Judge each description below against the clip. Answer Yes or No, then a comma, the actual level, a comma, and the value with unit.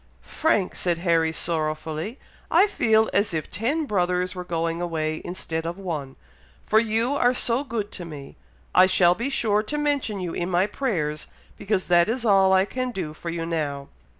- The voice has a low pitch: No, medium, 185 Hz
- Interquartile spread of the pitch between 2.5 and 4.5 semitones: No, average, 5.0 semitones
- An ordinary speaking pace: Yes, average, 180 wpm